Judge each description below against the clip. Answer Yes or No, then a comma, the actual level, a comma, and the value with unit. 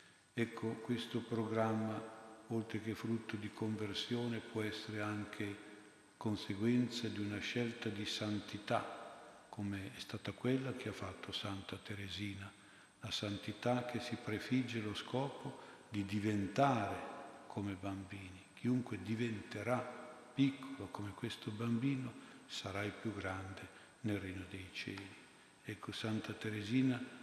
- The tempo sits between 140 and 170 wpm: No, average, 120 wpm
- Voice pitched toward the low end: Yes, low, 110 Hz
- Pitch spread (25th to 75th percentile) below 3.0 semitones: Yes, narrow, 2.4 semitones